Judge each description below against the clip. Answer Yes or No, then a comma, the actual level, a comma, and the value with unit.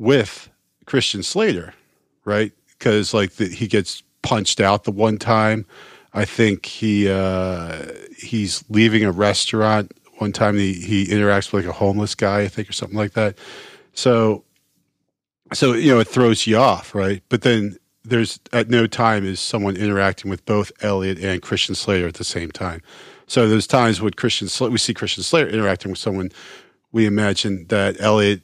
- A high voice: No, low, 105 Hz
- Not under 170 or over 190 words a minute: Yes, average, 175 wpm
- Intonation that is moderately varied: No, narrow, 2.3 semitones